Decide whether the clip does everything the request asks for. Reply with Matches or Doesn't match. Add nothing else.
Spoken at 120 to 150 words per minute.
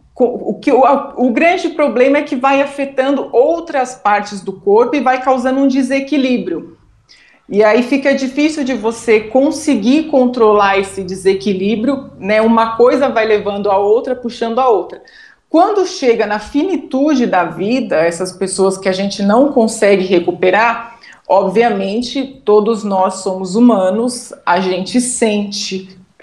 Matches